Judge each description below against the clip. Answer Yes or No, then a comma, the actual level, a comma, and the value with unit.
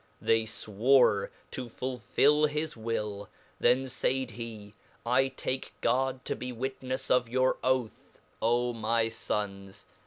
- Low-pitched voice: Yes, low, 120 Hz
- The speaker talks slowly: Yes, slow, 95 wpm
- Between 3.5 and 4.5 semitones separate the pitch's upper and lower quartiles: No, average, 2.7 semitones